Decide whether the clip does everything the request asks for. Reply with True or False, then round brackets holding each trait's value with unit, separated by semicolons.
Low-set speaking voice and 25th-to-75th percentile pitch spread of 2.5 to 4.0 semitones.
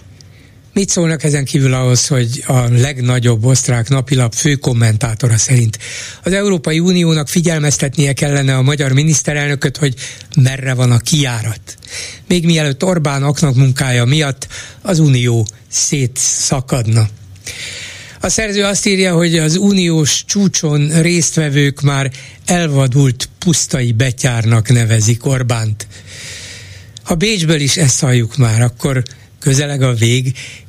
False (130 Hz; 4.5 semitones)